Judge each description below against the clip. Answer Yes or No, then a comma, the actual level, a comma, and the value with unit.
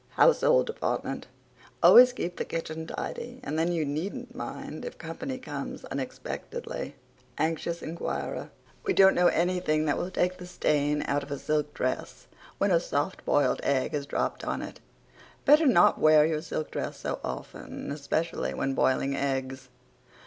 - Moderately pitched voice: Yes, medium, 160 Hz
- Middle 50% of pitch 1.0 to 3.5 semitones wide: No, average, 4.0 semitones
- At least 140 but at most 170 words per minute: Yes, average, 155 wpm